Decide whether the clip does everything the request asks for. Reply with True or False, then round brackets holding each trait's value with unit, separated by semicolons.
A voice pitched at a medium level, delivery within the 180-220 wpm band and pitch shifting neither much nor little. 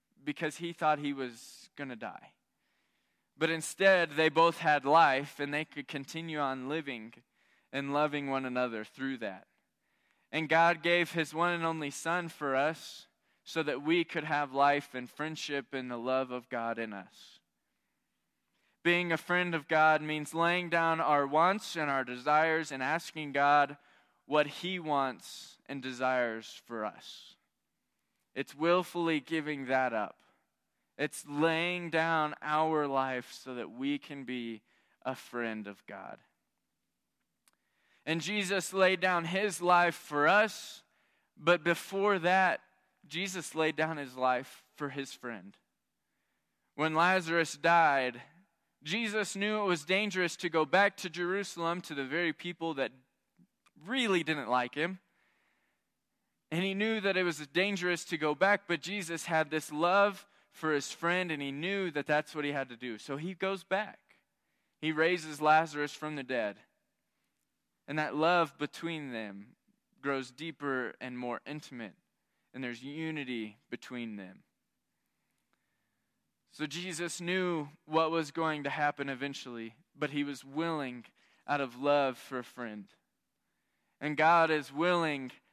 False (155 Hz; 145 wpm; 3.9 semitones)